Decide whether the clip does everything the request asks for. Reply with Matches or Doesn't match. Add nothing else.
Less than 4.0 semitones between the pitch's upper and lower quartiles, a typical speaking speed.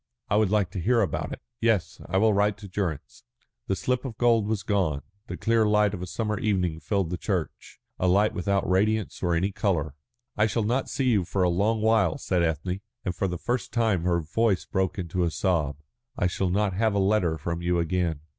Doesn't match